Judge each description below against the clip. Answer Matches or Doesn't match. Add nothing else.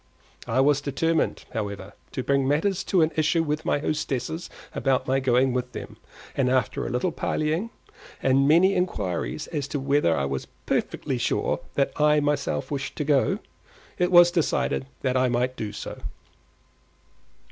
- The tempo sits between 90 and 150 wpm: Doesn't match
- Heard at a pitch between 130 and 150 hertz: Matches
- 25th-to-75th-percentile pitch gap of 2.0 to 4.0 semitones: Matches